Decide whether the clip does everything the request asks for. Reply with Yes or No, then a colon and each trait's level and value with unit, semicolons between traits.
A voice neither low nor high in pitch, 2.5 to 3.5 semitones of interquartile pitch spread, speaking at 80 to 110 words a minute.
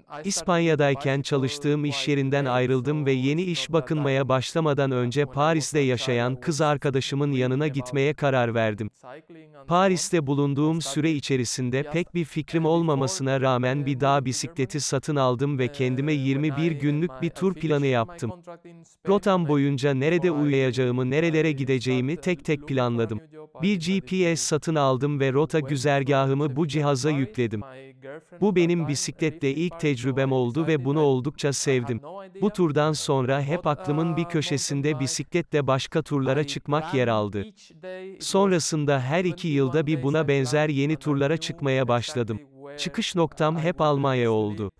No: medium, 145 Hz; average, 3.2 semitones; average, 135 wpm